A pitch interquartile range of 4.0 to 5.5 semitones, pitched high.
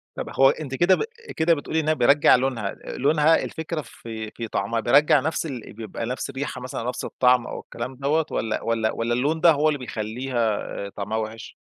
No: average, 4.5 semitones; low, 130 Hz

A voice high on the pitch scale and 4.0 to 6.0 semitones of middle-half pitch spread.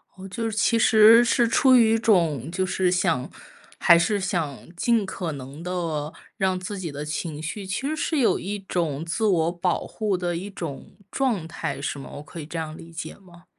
No: medium, 180 Hz; average, 4.3 semitones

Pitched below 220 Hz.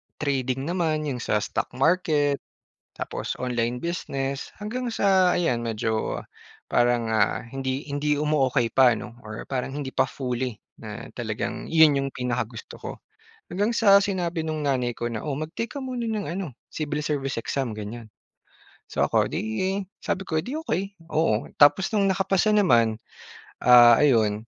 Yes: medium, 140 Hz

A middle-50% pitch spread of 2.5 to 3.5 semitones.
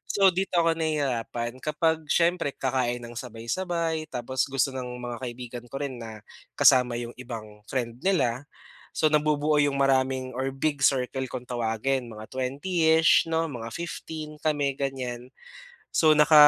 No: average, 4.1 semitones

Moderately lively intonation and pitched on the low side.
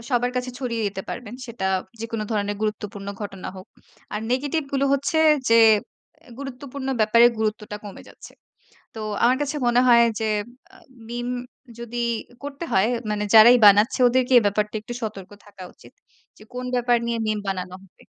No: average, 3.2 semitones; high, 230 Hz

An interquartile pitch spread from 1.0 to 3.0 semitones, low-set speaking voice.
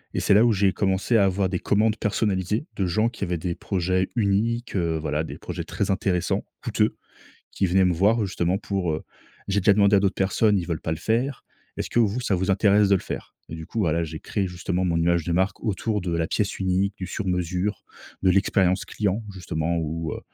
Yes: average, 2.7 semitones; very low, 95 Hz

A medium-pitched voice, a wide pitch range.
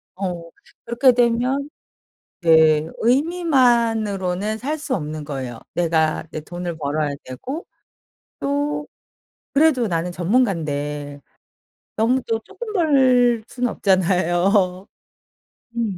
No: high, 205 Hz; wide, 7.4 semitones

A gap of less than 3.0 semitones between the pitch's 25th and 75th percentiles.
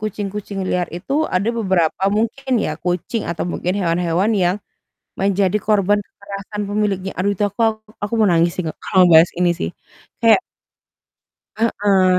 Yes: narrow, 2.5 semitones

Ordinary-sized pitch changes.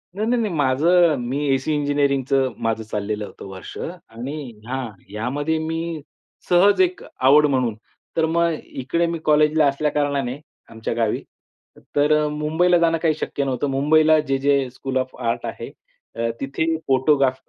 Yes: average, 3.6 semitones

